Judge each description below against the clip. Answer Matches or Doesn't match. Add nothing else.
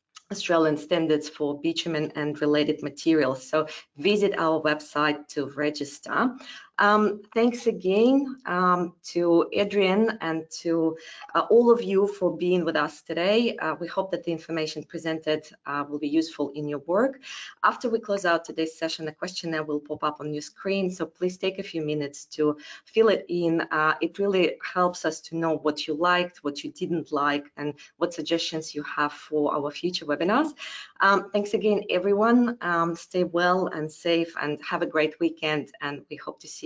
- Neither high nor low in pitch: Matches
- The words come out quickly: Doesn't match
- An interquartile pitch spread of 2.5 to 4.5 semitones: Matches